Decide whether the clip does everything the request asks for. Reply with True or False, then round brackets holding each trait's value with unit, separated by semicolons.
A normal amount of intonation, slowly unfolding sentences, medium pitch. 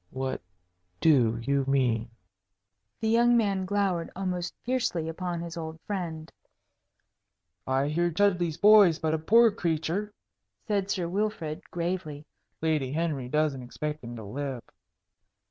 True (5.0 semitones; 130 wpm; 165 Hz)